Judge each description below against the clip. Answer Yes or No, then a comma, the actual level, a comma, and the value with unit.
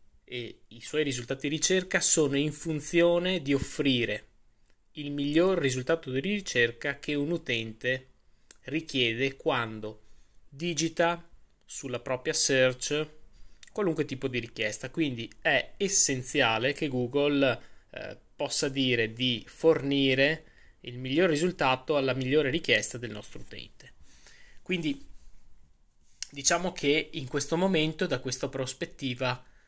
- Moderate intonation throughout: Yes, average, 4.3 semitones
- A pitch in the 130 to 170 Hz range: Yes, medium, 140 Hz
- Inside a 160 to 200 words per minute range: No, slow, 115 wpm